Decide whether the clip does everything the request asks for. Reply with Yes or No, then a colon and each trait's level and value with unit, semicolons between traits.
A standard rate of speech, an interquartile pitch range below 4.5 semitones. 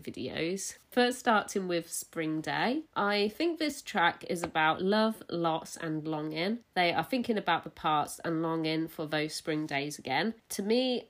No: average, 170 wpm; wide, 5.5 semitones